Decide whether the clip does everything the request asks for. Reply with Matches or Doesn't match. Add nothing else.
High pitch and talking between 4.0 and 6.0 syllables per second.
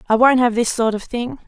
Matches